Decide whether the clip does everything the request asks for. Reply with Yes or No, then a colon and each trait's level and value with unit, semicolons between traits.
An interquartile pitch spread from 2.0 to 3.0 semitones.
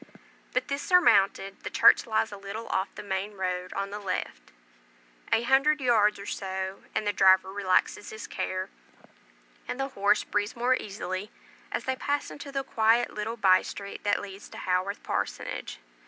No: average, 3.7 semitones